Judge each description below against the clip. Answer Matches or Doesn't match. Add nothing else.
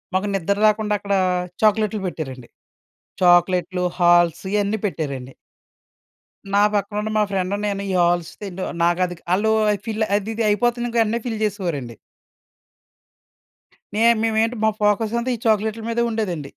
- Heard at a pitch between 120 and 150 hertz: Doesn't match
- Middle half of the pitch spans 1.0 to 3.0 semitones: Doesn't match